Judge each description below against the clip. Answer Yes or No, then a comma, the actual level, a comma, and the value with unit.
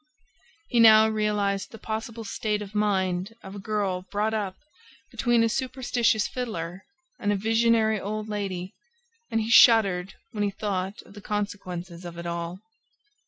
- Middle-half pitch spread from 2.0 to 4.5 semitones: Yes, narrow, 2.6 semitones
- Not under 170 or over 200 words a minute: No, average, 155 wpm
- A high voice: Yes, high, 210 Hz